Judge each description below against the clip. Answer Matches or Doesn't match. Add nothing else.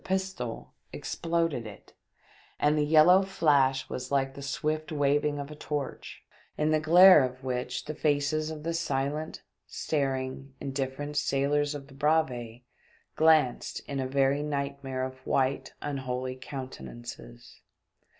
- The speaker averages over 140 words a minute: Doesn't match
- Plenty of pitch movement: Doesn't match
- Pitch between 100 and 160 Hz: Matches